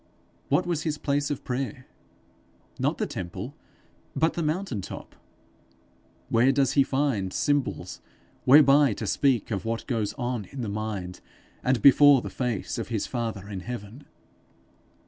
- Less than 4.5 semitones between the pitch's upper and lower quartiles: No, average, 4.8 semitones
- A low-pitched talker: Yes, low, 125 Hz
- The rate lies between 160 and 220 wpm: No, average, 145 wpm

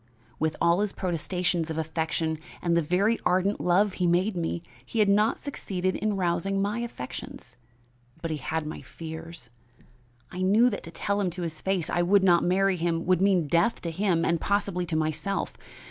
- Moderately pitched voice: Yes, medium, 180 Hz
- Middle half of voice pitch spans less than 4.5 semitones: Yes, average, 3.0 semitones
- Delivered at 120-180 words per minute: No, average, 190 wpm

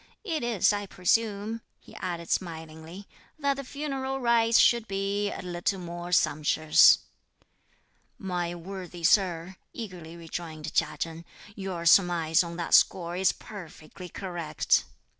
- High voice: No, medium, 180 Hz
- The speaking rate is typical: No, slow, 125 wpm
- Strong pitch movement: No, average, 3.5 semitones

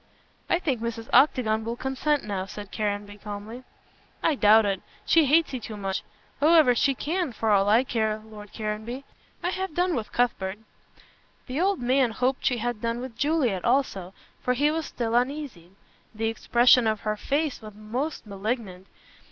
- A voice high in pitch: Yes, high, 235 Hz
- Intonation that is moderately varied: Yes, average, 4.4 semitones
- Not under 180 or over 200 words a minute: No, average, 170 wpm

